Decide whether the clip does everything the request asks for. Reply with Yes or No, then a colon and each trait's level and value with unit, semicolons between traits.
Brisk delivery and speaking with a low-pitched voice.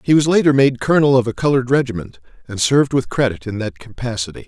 Yes: fast, 215 wpm; low, 125 Hz